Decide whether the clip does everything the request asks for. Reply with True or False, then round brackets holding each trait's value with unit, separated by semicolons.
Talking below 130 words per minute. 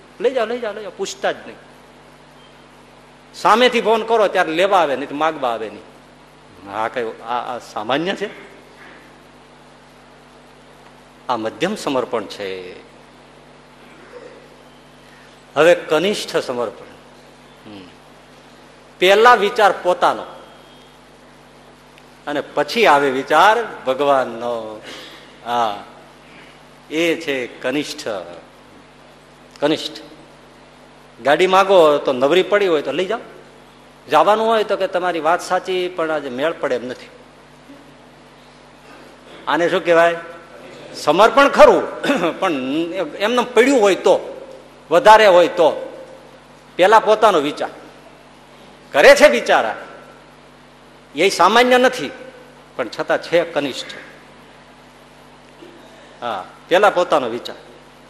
True (100 wpm)